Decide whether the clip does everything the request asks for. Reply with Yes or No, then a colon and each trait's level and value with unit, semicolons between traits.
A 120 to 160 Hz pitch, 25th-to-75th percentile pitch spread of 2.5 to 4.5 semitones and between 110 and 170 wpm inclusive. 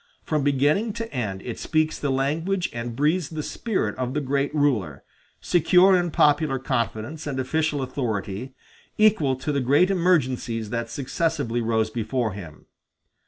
No: medium, 140 Hz; average, 5.1 semitones; average, 150 wpm